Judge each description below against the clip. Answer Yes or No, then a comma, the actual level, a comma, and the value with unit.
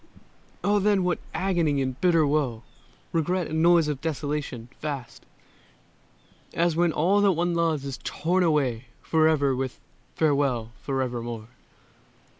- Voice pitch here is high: No, medium, 155 Hz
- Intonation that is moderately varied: Yes, average, 4.4 semitones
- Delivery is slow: Yes, slow, 125 wpm